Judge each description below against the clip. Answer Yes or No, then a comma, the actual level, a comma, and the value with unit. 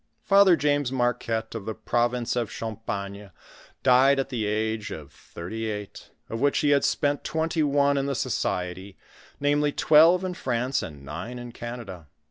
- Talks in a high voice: No, low, 120 Hz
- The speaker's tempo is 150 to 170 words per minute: Yes, average, 160 wpm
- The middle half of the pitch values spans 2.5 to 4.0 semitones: No, average, 4.9 semitones